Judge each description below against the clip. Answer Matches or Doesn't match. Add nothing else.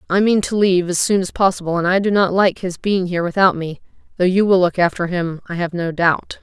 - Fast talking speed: Matches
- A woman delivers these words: Matches